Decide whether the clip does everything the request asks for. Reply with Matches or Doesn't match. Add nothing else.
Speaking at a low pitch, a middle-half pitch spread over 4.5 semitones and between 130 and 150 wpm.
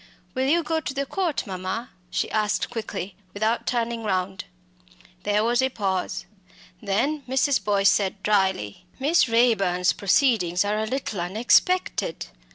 Doesn't match